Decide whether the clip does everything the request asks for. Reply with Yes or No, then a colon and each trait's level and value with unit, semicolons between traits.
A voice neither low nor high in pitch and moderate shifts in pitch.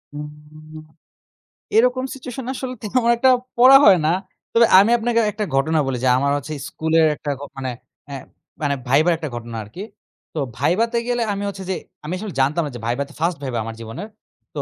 No: medium, 160 Hz; wide, 8.3 semitones